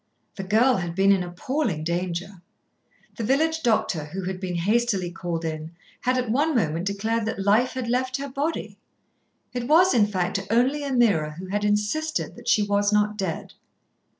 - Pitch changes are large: Yes, wide, 5.7 semitones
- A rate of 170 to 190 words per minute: Yes, average, 175 wpm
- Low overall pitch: No, high, 210 Hz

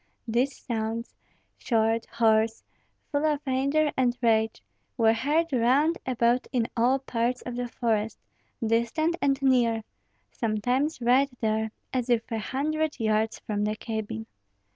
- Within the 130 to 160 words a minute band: Yes, slow, 135 wpm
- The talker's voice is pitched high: Yes, high, 240 Hz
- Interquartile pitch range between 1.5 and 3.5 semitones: Yes, average, 3.2 semitones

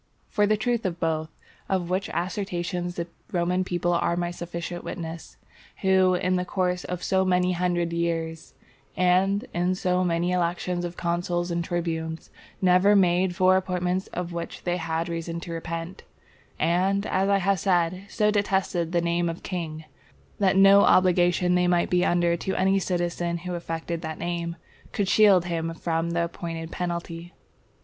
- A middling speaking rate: Yes, average, 165 wpm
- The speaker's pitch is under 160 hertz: No, medium, 175 Hz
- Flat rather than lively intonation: Yes, narrow, 1.5 semitones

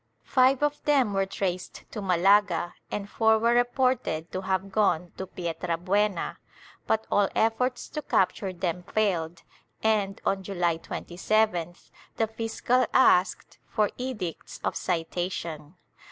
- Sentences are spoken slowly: Yes, slow, 125 wpm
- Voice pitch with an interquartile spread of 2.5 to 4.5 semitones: Yes, average, 4.0 semitones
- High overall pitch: Yes, high, 195 Hz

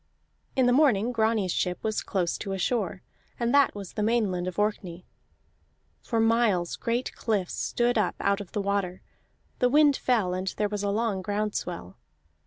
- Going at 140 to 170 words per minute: No, average, 180 wpm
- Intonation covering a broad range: No, average, 3.8 semitones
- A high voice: Yes, high, 210 Hz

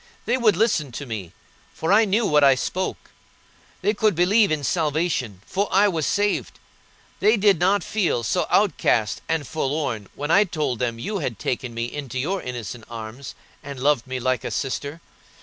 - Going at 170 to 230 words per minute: Yes, average, 180 wpm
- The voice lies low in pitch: No, medium, 150 Hz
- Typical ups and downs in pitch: No, wide, 7.5 semitones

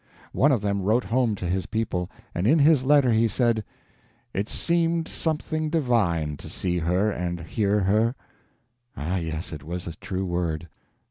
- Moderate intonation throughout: No, wide, 6.2 semitones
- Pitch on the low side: Yes, low, 100 Hz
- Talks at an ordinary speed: Yes, average, 175 wpm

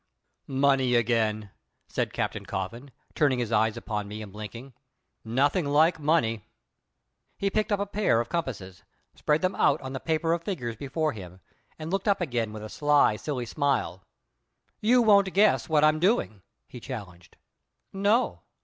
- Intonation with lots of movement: Yes, wide, 7.0 semitones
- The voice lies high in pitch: No, low, 135 Hz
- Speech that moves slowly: No, average, 160 wpm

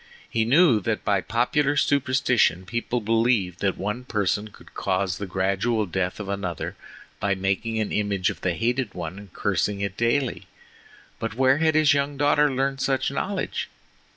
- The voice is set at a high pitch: No, low, 110 Hz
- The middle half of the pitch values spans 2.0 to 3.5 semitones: No, average, 5.2 semitones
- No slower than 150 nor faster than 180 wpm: Yes, average, 165 wpm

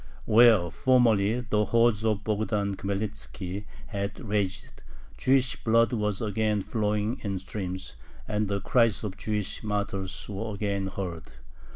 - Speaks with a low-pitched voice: Yes, low, 105 Hz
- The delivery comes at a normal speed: No, slow, 130 wpm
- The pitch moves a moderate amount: No, narrow, 2.0 semitones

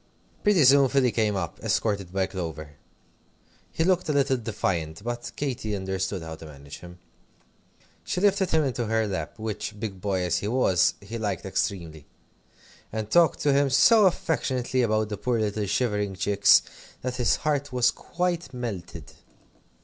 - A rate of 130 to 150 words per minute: No, average, 160 wpm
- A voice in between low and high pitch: No, low, 110 Hz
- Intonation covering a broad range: Yes, wide, 5.8 semitones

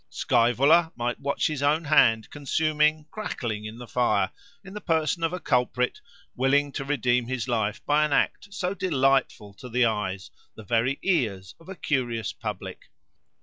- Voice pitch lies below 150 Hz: Yes, low, 135 Hz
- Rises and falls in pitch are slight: No, average, 4.9 semitones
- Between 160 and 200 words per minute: Yes, average, 165 wpm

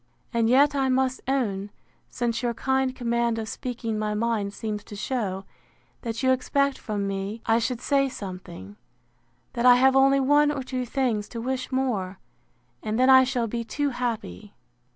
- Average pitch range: Yes, average, 3.5 semitones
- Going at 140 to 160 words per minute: No, average, 175 wpm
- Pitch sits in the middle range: No, high, 240 Hz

